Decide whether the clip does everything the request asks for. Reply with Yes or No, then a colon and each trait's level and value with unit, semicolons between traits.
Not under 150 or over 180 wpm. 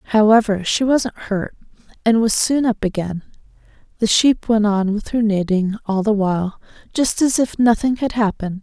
Yes: average, 175 wpm